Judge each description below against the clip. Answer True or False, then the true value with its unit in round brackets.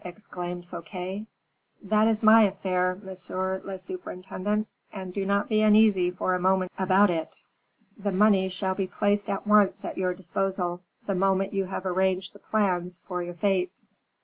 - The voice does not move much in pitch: True (1.9 semitones)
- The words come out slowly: False (165 wpm)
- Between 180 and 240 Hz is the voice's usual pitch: True (190 Hz)